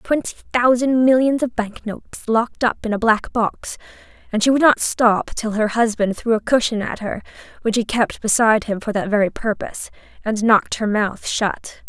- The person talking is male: No, female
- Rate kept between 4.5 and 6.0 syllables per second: No, 4.0 syllables/s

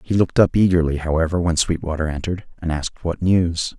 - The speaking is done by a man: Yes, male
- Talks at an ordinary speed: Yes, average, 190 wpm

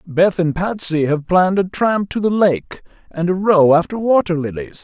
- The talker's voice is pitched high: No, medium, 180 Hz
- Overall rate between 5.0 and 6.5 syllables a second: No, 4.8 syllables/s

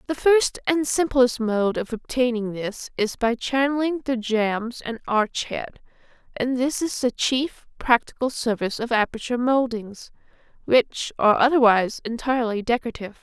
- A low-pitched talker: No, high, 240 Hz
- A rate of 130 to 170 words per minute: Yes, average, 140 wpm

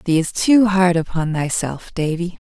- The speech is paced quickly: No, average, 170 wpm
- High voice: No, medium, 175 Hz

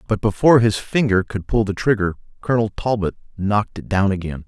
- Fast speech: No, average, 190 wpm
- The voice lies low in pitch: Yes, low, 105 Hz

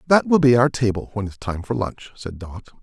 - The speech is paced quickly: Yes, fast, 255 wpm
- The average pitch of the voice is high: No, low, 115 Hz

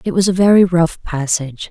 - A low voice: No, medium, 170 Hz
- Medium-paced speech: No, fast, 210 wpm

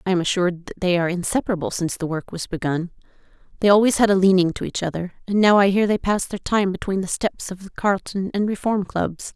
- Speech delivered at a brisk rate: Yes, fast, 235 wpm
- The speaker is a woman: Yes, female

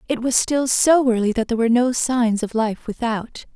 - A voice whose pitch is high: Yes, high, 240 Hz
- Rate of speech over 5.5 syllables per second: No, 5.2 syllables/s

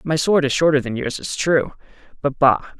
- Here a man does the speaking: Yes, male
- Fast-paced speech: Yes, fast, 215 wpm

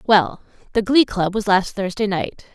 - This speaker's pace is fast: No, average, 165 wpm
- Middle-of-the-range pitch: No, high, 200 Hz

